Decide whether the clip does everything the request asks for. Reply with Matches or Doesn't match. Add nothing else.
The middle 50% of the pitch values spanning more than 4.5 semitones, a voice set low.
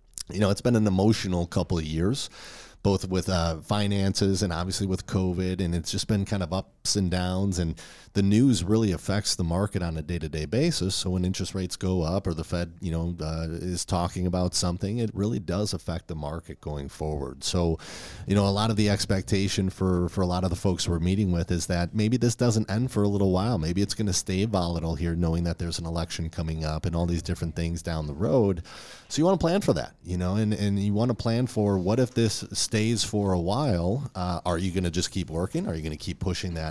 Doesn't match